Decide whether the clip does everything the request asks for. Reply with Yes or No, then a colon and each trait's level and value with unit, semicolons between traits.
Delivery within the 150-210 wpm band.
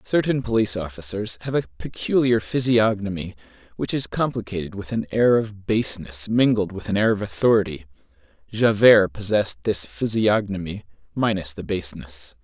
No: slow, 135 wpm